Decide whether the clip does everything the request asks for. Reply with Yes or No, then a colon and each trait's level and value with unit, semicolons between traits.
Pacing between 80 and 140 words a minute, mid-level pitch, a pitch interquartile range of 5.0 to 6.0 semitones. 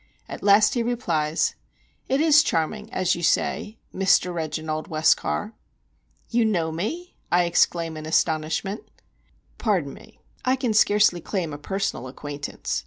Yes: slow, 135 wpm; medium, 180 Hz; average, 5.3 semitones